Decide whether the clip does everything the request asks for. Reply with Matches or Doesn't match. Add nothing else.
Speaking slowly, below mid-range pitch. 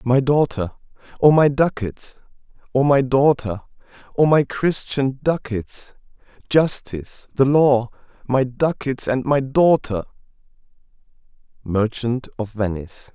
Matches